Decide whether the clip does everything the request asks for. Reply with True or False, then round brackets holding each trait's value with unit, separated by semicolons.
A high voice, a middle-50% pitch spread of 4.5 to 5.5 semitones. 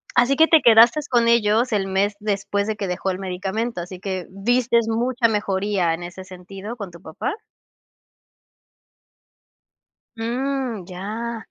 False (210 Hz; 3.7 semitones)